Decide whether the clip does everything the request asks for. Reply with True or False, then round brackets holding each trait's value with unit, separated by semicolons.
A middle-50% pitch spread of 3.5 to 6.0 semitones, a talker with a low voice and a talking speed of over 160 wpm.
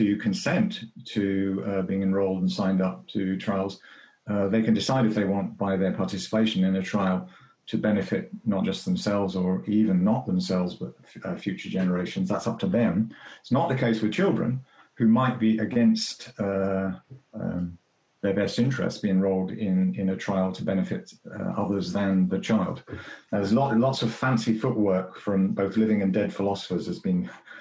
False (2.9 semitones; 100 Hz; 185 wpm)